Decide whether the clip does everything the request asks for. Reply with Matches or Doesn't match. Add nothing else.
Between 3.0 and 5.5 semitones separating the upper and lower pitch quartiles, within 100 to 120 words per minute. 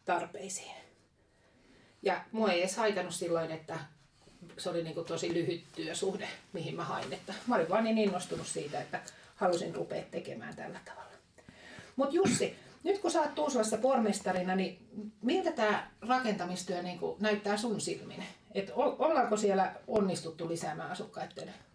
Doesn't match